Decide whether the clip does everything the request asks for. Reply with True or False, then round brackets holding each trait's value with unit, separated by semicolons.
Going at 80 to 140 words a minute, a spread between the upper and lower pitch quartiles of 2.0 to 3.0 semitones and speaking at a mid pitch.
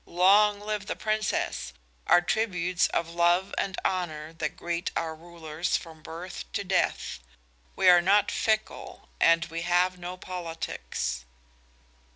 True (135 wpm; 2.4 semitones; 175 Hz)